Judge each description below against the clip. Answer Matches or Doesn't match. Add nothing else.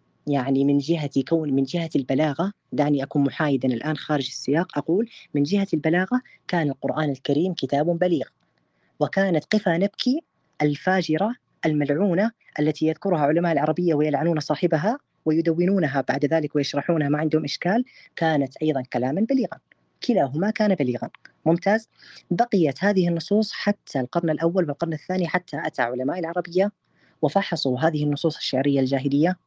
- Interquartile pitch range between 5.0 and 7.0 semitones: Doesn't match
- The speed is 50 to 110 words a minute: Doesn't match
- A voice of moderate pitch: Matches